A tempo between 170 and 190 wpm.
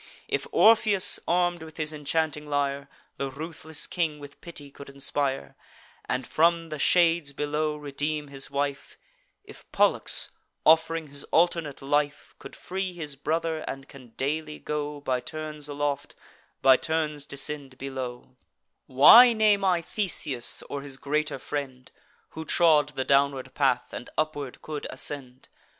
No: average, 140 wpm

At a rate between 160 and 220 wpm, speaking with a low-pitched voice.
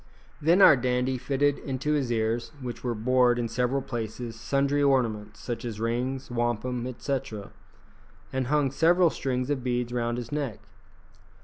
No: average, 150 wpm; low, 125 Hz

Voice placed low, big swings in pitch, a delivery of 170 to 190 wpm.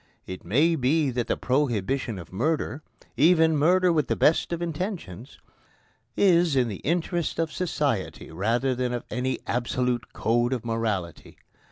No: low, 130 Hz; wide, 5.7 semitones; average, 145 wpm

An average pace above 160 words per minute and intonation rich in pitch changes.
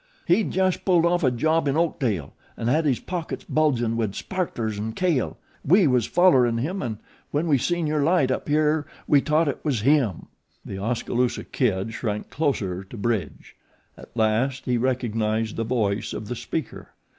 Yes: average, 175 wpm; wide, 5.7 semitones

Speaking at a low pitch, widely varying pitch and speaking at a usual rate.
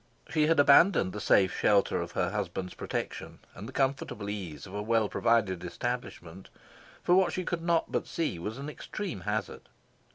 Yes: low, 110 Hz; wide, 7.8 semitones; average, 175 wpm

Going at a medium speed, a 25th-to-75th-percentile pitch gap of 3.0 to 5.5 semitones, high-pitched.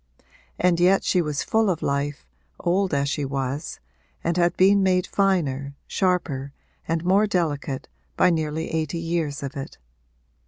No: average, 150 wpm; average, 4.3 semitones; medium, 165 Hz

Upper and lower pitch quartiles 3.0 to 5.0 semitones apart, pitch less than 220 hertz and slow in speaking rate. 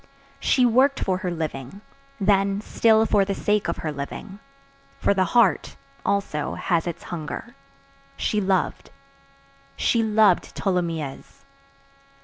No: wide, 5.5 semitones; medium, 185 Hz; slow, 115 wpm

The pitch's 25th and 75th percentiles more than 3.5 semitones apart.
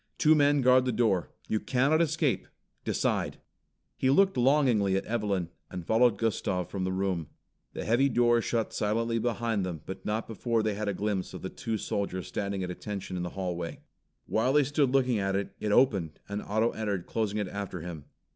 Yes: average, 4.2 semitones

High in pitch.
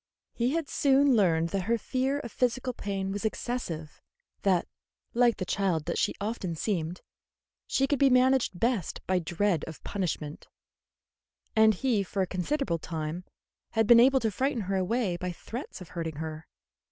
Yes: high, 200 Hz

